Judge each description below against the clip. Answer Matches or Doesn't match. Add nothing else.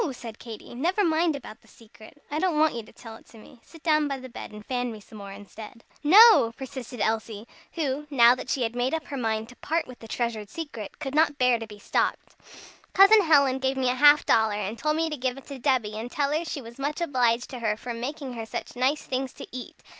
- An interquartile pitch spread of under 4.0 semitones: Doesn't match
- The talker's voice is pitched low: Doesn't match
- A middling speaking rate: Doesn't match